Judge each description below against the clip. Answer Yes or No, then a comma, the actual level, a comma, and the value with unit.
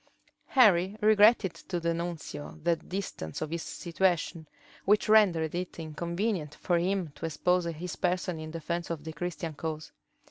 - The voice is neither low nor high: Yes, medium, 170 Hz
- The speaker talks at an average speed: Yes, average, 150 wpm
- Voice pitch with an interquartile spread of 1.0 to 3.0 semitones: Yes, narrow, 2.5 semitones